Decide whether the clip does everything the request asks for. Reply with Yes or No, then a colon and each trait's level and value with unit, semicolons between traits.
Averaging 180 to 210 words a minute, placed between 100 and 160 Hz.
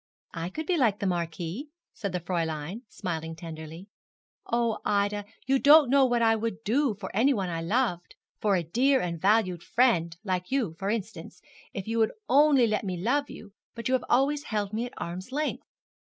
No: average, 190 wpm; high, 210 Hz